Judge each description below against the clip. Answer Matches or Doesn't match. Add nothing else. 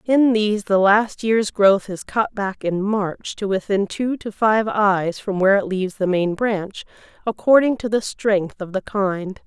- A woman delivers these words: Matches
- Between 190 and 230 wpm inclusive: Matches